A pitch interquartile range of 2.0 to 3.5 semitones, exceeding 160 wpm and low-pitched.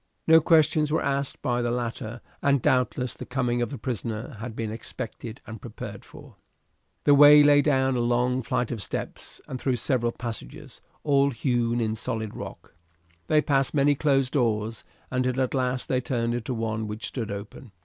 Yes: average, 3.0 semitones; average, 180 wpm; low, 125 Hz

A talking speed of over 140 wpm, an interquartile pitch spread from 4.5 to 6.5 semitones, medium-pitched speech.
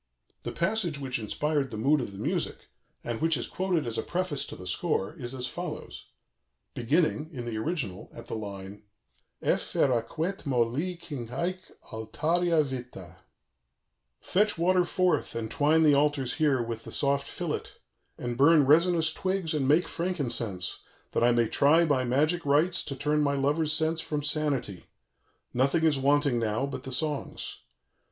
Yes: average, 165 wpm; average, 5.0 semitones; medium, 145 Hz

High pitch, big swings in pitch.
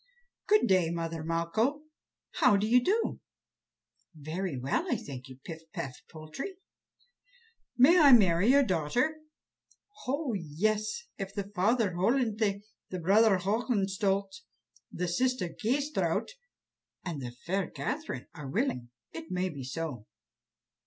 Yes: high, 195 Hz; wide, 7.0 semitones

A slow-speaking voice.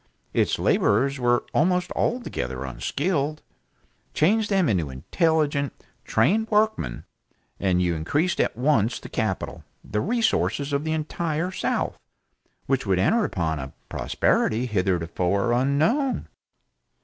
Yes: slow, 115 wpm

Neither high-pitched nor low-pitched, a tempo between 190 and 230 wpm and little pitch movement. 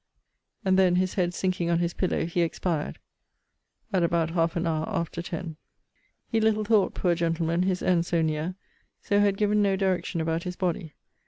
No: medium, 175 Hz; average, 180 wpm; narrow, 2.2 semitones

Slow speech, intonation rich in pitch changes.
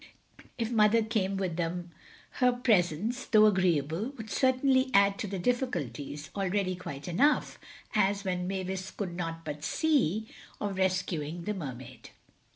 No: slow, 130 wpm; average, 4.2 semitones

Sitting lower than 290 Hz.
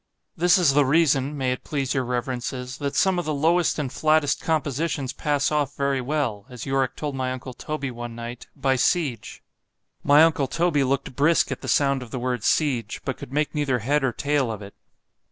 Yes: medium, 140 Hz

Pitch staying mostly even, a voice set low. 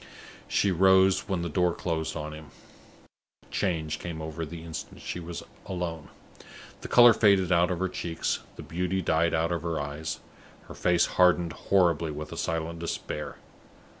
Yes: narrow, 2.1 semitones; very low, 85 Hz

